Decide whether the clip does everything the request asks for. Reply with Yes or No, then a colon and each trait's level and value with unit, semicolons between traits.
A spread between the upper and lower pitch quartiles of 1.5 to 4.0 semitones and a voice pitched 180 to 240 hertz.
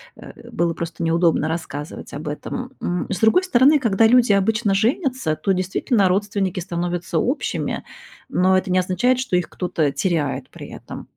No: average, 5.0 semitones; medium, 185 Hz